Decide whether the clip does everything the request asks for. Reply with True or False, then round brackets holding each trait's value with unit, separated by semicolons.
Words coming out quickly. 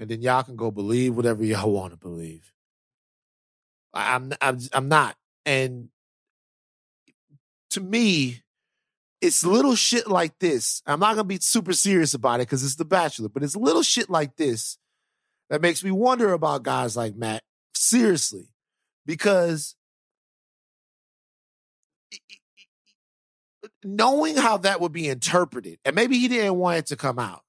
False (145 wpm)